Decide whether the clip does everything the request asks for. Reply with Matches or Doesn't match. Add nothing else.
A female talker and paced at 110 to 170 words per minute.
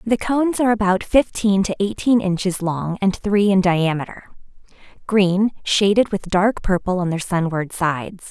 Matches